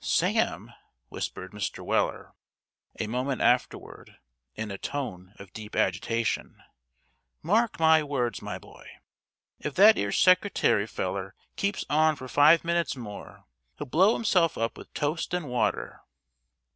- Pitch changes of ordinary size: No, wide, 7.6 semitones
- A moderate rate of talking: No, slow, 130 wpm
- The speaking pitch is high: No, medium, 140 Hz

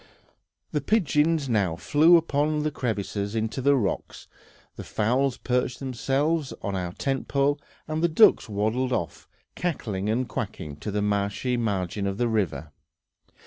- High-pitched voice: No, low, 125 Hz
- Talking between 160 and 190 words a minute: No, average, 145 wpm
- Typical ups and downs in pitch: No, wide, 6.0 semitones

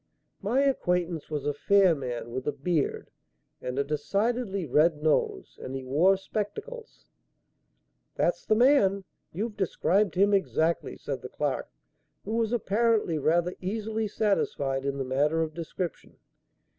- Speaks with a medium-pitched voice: Yes, medium, 180 Hz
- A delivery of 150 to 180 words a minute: No, average, 140 wpm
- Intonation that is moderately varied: No, wide, 6.1 semitones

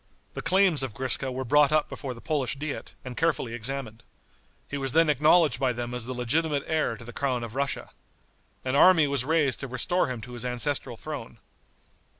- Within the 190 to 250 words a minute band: Yes, average, 195 wpm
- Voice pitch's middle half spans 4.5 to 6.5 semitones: No, average, 3.6 semitones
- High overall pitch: No, low, 135 Hz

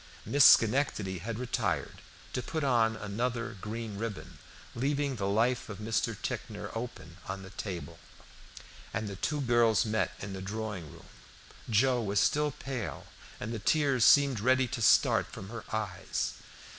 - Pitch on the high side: No, low, 115 Hz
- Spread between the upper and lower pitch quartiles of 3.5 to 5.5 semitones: Yes, average, 3.9 semitones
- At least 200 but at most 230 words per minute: No, average, 155 wpm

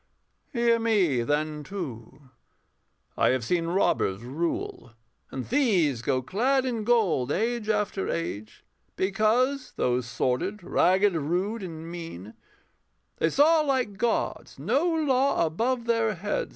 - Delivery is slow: Yes, slow, 125 wpm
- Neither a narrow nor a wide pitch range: No, wide, 7.9 semitones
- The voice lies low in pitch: No, high, 190 Hz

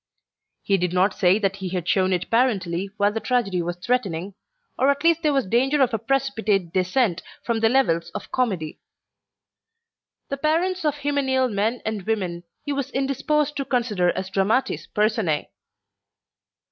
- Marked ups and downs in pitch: Yes, wide, 6.3 semitones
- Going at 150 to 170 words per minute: Yes, average, 160 wpm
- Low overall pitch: No, high, 220 Hz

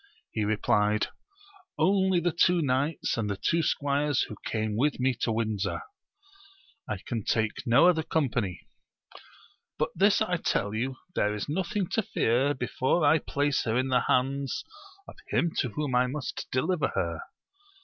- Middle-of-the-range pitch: No, low, 130 Hz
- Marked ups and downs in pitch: Yes, wide, 6.1 semitones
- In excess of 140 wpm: Yes, average, 160 wpm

